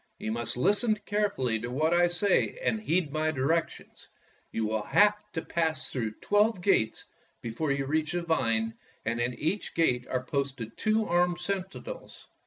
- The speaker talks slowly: No, average, 165 wpm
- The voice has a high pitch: No, medium, 155 Hz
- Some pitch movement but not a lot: No, wide, 7.1 semitones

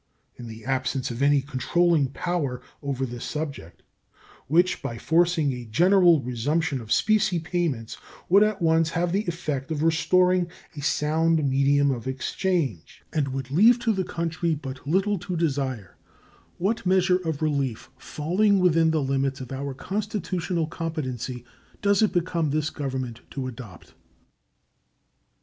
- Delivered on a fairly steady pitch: No, average, 4.8 semitones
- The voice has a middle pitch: Yes, medium, 155 Hz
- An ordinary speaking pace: Yes, average, 145 wpm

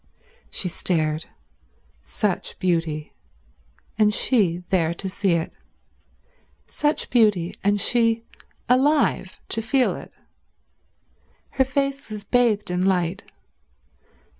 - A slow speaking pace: Yes, slow, 100 wpm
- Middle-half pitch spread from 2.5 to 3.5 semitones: No, wide, 5.6 semitones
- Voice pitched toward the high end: Yes, high, 205 Hz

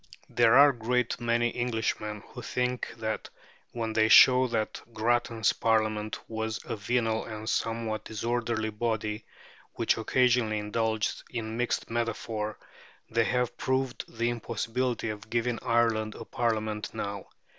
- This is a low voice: Yes, low, 115 Hz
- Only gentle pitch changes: Yes, narrow, 1.6 semitones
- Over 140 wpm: No, slow, 135 wpm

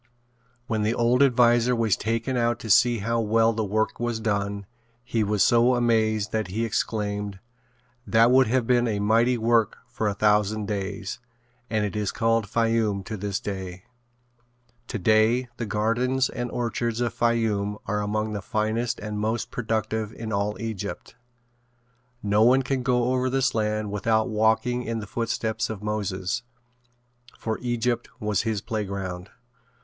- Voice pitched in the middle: No, low, 110 Hz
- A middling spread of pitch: No, narrow, 2.1 semitones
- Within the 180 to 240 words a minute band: No, average, 155 wpm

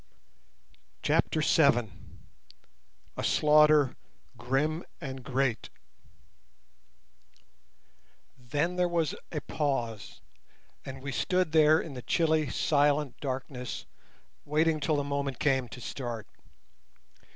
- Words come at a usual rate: No, slow, 95 wpm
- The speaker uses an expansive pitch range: No, average, 3.0 semitones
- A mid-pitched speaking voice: Yes, medium, 145 Hz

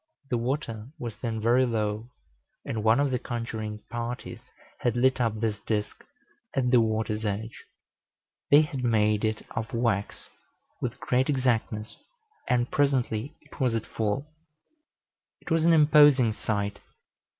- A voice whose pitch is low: Yes, low, 115 Hz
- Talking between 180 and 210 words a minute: No, average, 140 wpm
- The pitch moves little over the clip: No, average, 3.0 semitones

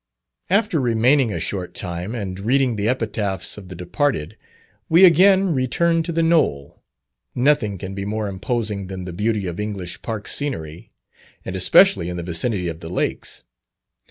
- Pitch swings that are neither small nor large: No, wide, 6.6 semitones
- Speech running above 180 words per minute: No, average, 160 wpm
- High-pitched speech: No, low, 105 Hz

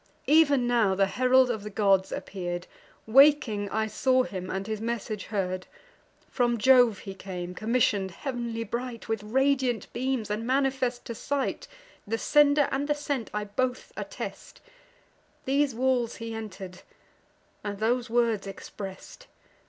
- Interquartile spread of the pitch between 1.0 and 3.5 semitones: No, average, 4.2 semitones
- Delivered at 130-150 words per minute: Yes, average, 140 wpm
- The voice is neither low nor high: No, high, 230 Hz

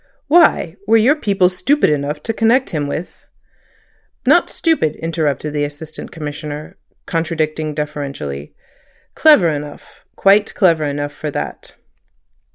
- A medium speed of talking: No, slow, 115 wpm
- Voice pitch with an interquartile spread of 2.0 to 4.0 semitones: No, average, 5.0 semitones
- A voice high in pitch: No, medium, 155 Hz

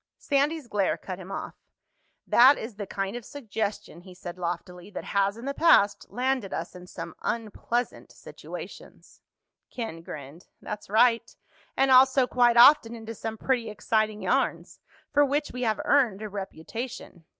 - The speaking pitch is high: Yes, high, 220 Hz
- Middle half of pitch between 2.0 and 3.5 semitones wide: No, average, 4.4 semitones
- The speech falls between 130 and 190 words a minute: Yes, average, 155 wpm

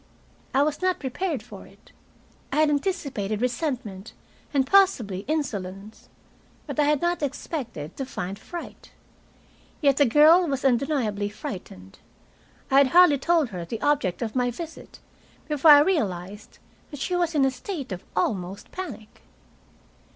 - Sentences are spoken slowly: No, average, 145 wpm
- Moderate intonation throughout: No, wide, 6.7 semitones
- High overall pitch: Yes, very high, 270 Hz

